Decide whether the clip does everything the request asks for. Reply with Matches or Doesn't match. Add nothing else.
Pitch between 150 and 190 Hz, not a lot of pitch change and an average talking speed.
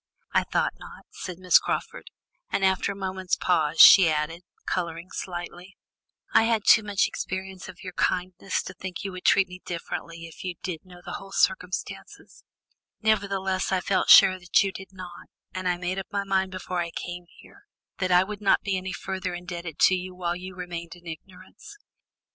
Matches